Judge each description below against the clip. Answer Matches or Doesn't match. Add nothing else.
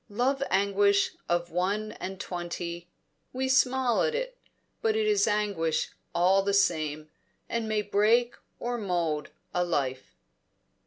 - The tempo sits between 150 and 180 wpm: Doesn't match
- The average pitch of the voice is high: Matches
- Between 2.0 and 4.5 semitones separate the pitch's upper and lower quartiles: Doesn't match